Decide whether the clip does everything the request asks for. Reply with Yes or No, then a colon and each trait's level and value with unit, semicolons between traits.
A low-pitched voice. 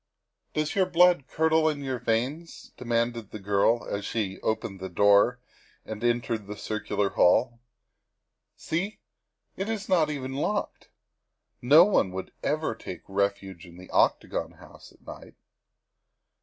Yes: low, 120 Hz